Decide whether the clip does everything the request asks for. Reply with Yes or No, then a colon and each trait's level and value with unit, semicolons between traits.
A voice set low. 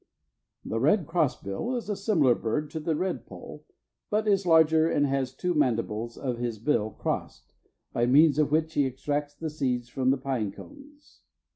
No: medium, 145 Hz